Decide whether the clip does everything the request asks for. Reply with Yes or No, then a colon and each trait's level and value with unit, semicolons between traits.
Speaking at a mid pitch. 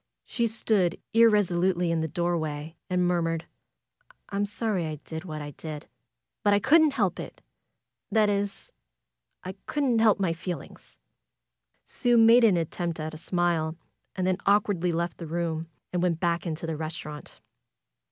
Yes: medium, 175 Hz